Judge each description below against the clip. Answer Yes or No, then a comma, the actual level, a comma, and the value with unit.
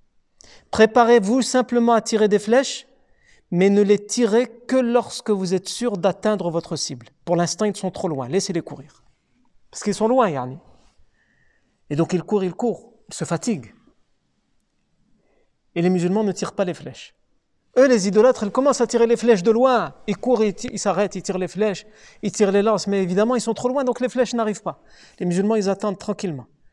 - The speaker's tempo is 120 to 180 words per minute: No, average, 200 wpm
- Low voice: No, high, 210 Hz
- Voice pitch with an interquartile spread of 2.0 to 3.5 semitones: No, average, 4.1 semitones